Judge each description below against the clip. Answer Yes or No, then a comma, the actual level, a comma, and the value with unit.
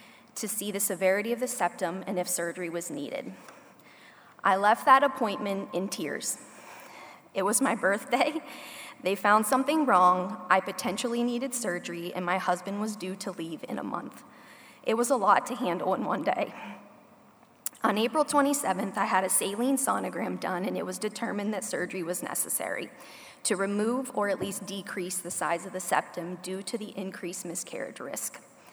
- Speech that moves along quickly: No, average, 175 wpm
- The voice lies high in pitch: Yes, high, 200 Hz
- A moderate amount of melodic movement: Yes, average, 4.1 semitones